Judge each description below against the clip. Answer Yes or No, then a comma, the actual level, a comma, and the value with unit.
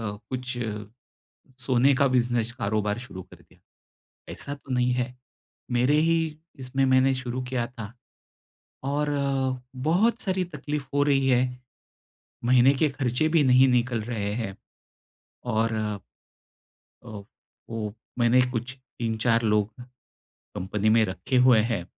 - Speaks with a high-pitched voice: No, low, 125 Hz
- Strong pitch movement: No, average, 2.9 semitones